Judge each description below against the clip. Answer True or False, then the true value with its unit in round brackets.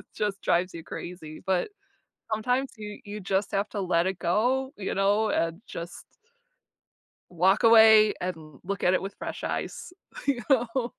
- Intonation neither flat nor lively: True (3.6 semitones)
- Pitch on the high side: True (200 Hz)